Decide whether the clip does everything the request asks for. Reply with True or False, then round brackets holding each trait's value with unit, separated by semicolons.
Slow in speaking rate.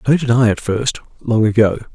False (185 wpm)